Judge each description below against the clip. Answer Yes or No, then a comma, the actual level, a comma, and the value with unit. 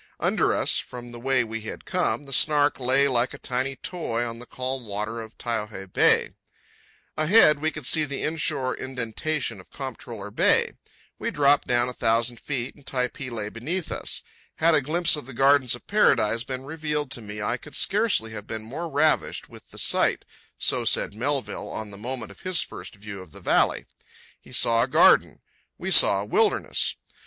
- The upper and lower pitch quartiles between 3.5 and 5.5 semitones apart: Yes, average, 4.4 semitones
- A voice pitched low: Yes, low, 125 Hz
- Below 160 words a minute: No, average, 185 wpm